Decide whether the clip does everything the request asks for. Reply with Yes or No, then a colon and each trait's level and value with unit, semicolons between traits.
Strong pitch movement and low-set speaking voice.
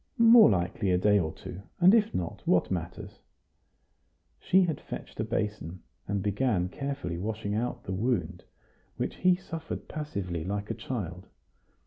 Yes: wide, 7.9 semitones; low, 105 Hz